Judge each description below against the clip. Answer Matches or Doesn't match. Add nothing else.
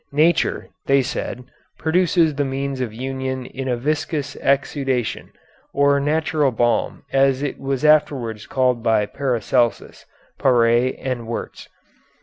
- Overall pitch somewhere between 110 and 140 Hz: Matches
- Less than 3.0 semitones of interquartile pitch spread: Matches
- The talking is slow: Matches